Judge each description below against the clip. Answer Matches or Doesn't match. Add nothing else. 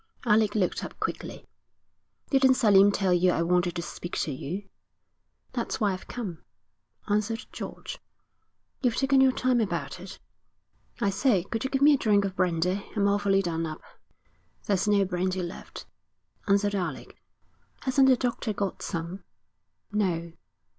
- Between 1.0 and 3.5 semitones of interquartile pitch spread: Doesn't match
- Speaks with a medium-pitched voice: Doesn't match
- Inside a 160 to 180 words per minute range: Doesn't match